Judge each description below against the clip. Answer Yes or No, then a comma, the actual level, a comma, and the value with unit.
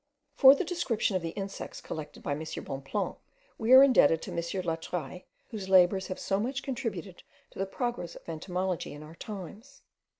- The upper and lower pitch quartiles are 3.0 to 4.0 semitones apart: No, average, 5.3 semitones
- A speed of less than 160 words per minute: No, average, 175 wpm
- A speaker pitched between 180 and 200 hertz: Yes, high, 190 Hz